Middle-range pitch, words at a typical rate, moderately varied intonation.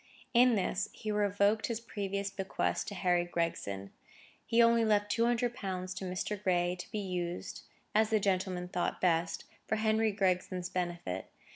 No: high, 195 Hz; average, 160 wpm; average, 3.3 semitones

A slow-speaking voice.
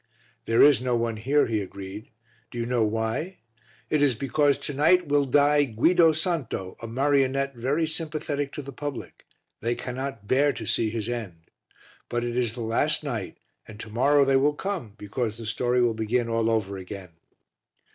No: average, 180 wpm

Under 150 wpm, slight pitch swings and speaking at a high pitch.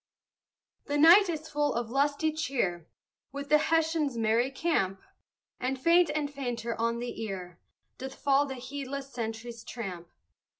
No: average, 140 wpm; average, 4.2 semitones; very high, 265 Hz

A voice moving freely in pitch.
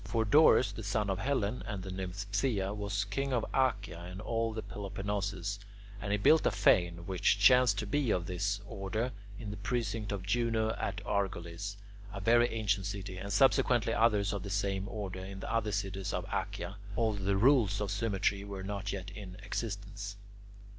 No: narrow, 2.4 semitones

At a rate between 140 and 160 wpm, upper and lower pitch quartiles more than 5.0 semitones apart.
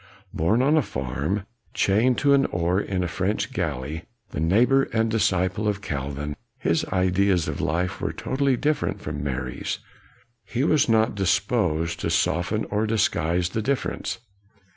Yes: average, 150 wpm; wide, 5.4 semitones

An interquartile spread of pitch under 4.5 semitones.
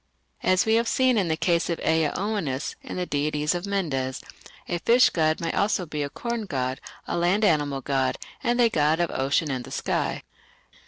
No: wide, 5.6 semitones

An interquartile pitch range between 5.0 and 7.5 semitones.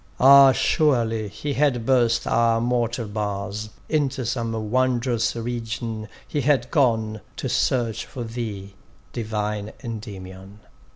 No: average, 2.9 semitones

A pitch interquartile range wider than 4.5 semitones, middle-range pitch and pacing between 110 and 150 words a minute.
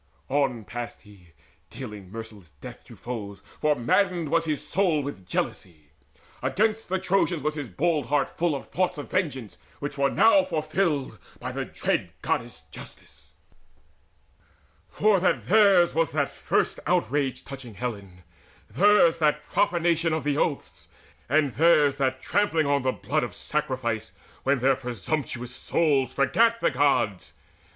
Yes: wide, 5.5 semitones; medium, 145 Hz; average, 145 wpm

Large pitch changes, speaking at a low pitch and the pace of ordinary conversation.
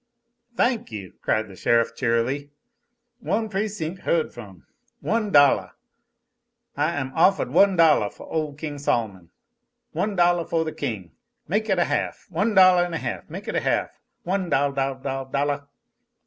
No: wide, 5.9 semitones; medium, 150 Hz; average, 160 wpm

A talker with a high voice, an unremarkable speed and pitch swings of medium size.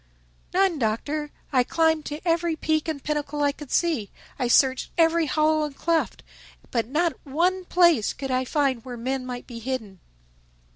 Yes: very high, 295 Hz; average, 165 wpm; average, 4.1 semitones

